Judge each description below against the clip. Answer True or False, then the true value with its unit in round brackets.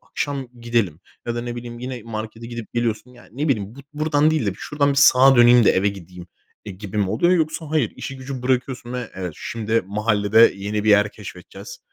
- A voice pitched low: True (120 Hz)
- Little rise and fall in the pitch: False (4.0 semitones)